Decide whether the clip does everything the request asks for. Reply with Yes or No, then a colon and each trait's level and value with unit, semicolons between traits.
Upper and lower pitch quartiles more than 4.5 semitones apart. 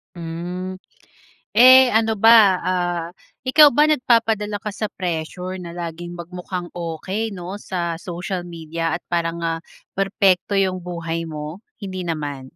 No: average, 3.0 semitones